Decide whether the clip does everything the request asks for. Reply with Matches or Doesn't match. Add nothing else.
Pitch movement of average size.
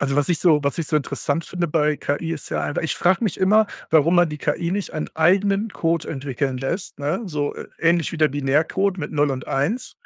Matches